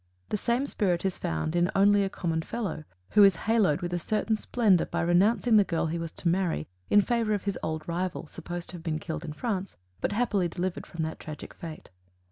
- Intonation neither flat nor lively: Yes, average, 3.8 semitones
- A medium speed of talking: No, fast, 220 wpm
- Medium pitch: Yes, medium, 180 Hz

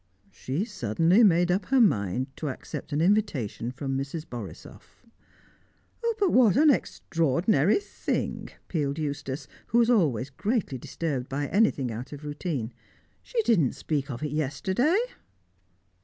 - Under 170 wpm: Yes, slow, 135 wpm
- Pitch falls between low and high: Yes, medium, 150 Hz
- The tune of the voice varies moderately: No, wide, 7.2 semitones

